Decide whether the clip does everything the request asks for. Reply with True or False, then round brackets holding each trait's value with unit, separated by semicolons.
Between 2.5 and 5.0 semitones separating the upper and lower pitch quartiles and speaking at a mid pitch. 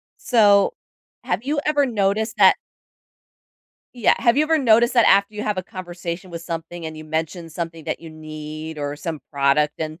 False (5.4 semitones; 175 Hz)